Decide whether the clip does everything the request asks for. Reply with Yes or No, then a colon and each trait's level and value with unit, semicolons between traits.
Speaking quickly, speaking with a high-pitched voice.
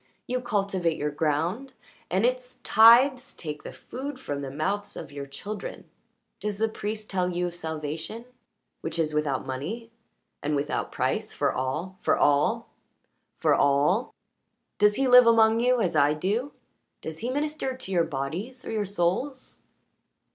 No: average, 155 wpm; high, 195 Hz